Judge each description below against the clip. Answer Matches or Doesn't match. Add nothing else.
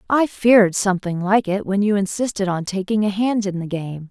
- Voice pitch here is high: Matches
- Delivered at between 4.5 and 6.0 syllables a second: Matches